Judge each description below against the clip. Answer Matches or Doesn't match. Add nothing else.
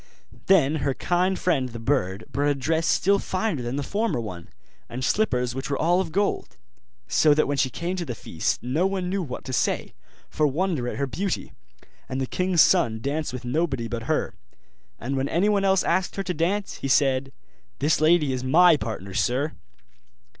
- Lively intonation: Matches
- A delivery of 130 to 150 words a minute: Doesn't match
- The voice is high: Doesn't match